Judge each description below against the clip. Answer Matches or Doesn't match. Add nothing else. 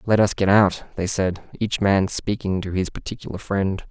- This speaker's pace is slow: Doesn't match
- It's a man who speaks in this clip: Matches